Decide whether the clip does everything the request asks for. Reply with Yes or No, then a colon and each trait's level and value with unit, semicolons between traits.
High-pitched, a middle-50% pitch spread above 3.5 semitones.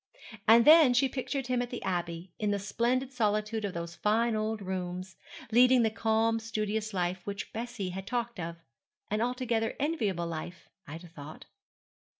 Yes: high, 215 Hz; average, 4.5 semitones